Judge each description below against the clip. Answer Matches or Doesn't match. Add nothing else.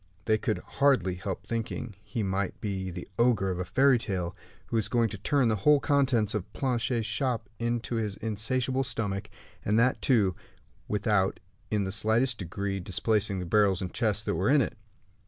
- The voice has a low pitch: Matches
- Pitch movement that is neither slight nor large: Matches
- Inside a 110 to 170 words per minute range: Doesn't match